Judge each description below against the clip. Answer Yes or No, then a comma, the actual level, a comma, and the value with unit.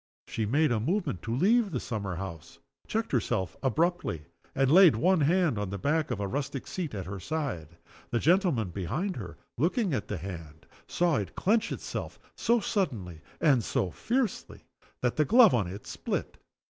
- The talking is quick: No, average, 175 wpm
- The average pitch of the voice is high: No, low, 130 Hz